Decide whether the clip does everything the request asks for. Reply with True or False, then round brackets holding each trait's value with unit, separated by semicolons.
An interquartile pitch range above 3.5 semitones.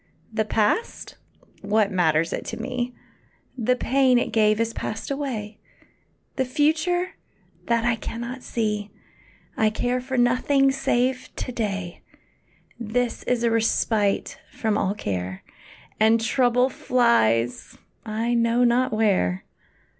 False (3.0 semitones)